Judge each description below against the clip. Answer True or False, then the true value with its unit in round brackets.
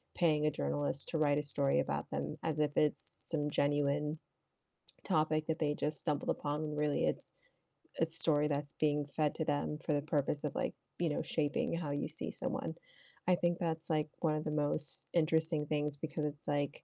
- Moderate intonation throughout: False (1.3 semitones)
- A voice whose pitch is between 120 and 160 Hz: True (150 Hz)